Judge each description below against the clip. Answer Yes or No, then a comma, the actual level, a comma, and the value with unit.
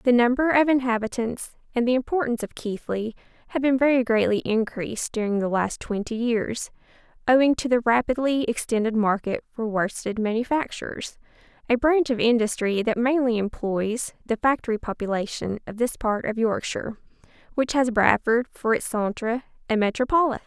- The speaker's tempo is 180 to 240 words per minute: No, average, 150 wpm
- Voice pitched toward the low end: No, high, 235 Hz